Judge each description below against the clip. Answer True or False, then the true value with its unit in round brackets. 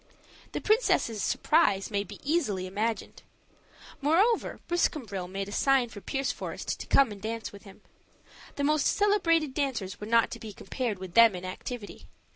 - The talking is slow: False (160 wpm)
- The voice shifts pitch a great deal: True (6.6 semitones)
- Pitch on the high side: True (230 Hz)